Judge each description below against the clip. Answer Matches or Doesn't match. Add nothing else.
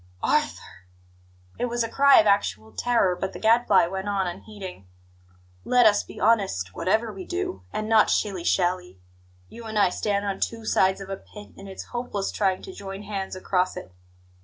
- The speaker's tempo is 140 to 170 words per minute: Doesn't match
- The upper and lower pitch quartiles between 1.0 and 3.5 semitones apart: Matches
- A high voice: Matches